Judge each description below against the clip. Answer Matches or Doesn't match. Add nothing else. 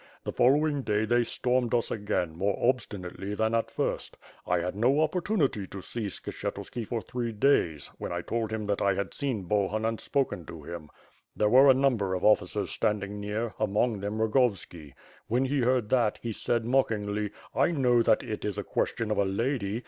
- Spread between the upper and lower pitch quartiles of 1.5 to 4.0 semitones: Matches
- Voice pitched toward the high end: Doesn't match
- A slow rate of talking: Doesn't match